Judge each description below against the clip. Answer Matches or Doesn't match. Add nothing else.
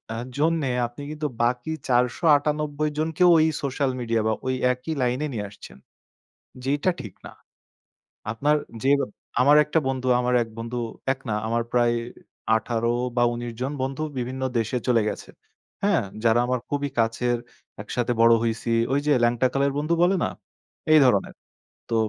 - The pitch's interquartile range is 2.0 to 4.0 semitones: Matches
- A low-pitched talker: Matches